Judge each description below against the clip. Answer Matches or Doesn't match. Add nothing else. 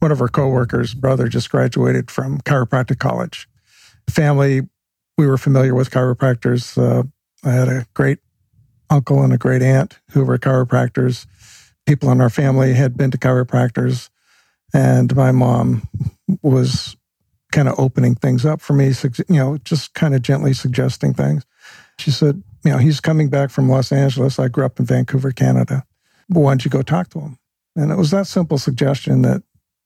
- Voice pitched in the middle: Doesn't match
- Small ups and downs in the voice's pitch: Matches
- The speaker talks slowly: Doesn't match